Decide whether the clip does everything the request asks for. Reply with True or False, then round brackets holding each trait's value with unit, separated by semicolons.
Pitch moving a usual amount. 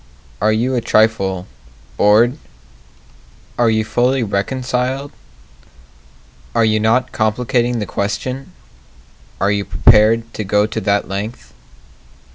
True (3.0 semitones)